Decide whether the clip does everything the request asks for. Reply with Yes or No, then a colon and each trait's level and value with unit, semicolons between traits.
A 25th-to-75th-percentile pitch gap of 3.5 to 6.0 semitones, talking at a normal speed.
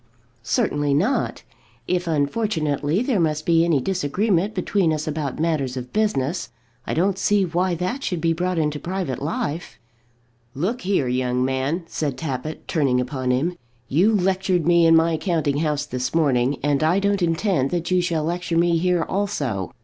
Yes: average, 4.1 semitones; average, 165 wpm